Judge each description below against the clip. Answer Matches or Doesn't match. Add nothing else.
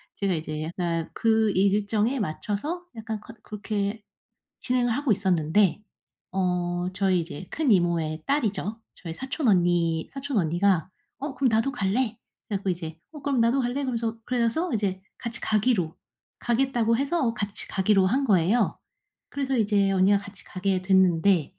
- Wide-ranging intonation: Doesn't match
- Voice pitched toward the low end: Doesn't match